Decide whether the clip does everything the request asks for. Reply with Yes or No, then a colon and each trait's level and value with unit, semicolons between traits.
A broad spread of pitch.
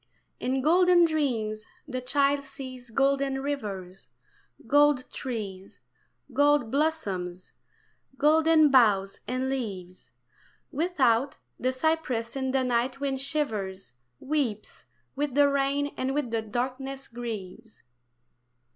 No: average, 4.1 semitones